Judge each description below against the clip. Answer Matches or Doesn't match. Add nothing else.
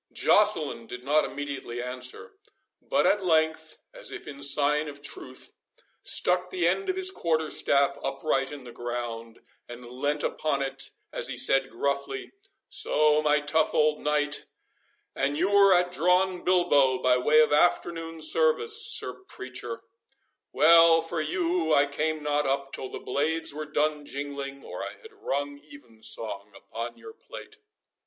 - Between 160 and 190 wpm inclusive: Doesn't match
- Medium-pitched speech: Matches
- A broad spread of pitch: Doesn't match